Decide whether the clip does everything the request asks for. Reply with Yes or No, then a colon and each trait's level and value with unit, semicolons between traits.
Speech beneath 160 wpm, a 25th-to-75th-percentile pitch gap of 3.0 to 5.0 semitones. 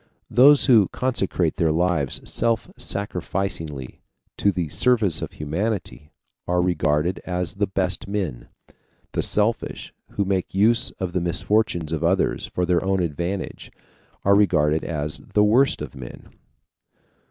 Yes: slow, 135 wpm; average, 3.9 semitones